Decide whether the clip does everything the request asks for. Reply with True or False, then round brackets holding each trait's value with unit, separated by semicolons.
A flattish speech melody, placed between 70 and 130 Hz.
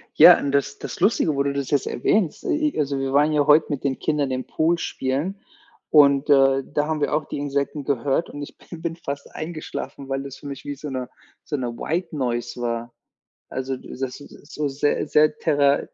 False (2.1 semitones; 140 Hz)